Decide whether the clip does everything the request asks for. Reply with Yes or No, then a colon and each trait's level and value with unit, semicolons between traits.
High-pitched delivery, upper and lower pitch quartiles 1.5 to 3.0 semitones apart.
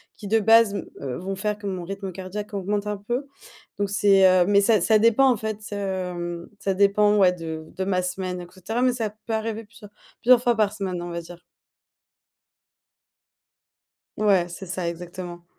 Yes: high, 195 Hz; average, 2.7 semitones